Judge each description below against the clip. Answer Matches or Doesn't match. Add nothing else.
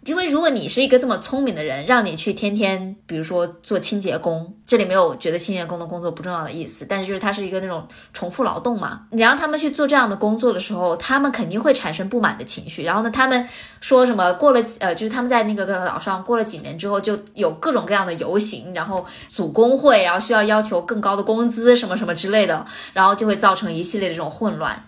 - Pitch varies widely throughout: Doesn't match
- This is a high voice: Matches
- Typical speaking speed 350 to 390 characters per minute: Matches